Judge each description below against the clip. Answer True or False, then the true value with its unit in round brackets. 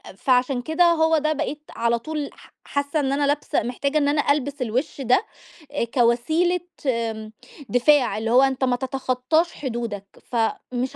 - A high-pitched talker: True (265 Hz)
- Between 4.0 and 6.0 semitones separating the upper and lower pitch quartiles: False (3.6 semitones)